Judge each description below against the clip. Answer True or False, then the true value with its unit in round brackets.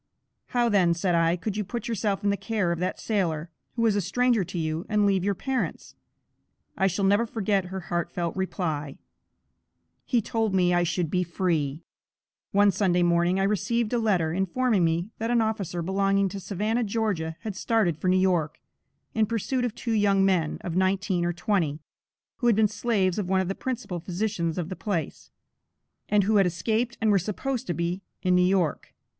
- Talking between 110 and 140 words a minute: False (195 wpm)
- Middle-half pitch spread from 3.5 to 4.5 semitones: True (3.8 semitones)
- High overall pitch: True (195 Hz)